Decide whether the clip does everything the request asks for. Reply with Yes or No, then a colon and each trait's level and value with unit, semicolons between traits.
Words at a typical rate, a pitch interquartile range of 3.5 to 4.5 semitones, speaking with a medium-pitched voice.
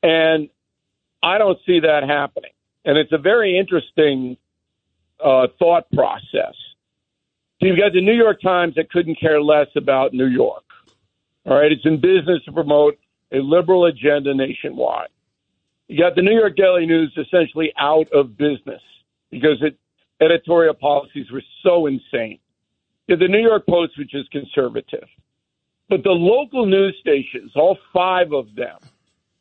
Yes: average, 155 wpm; average, 4.2 semitones; medium, 160 Hz